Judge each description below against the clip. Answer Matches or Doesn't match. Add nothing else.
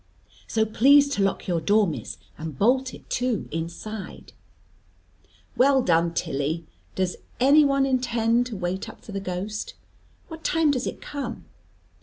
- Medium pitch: Doesn't match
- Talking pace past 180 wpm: Doesn't match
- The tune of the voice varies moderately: Doesn't match